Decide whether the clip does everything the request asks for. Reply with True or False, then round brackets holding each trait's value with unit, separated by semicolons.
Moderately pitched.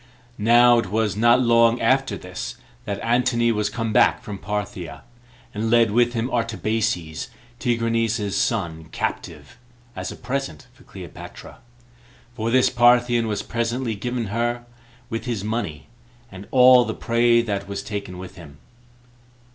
False (115 Hz)